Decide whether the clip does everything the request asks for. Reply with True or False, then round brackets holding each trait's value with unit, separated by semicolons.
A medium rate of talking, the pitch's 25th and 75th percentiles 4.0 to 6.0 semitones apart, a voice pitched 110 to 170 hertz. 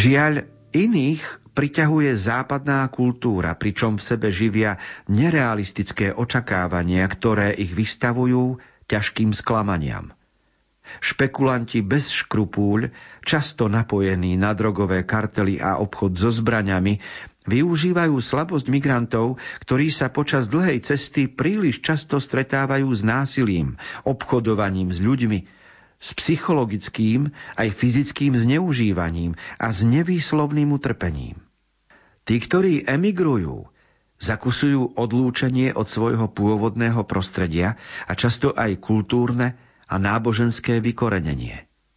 False (100 wpm; 4.7 semitones; 120 Hz)